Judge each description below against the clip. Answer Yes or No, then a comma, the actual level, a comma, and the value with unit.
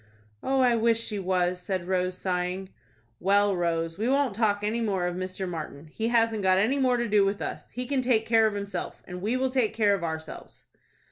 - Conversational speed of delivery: No, fast, 215 wpm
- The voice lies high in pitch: Yes, high, 200 Hz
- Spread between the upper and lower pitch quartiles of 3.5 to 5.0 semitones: Yes, average, 4.0 semitones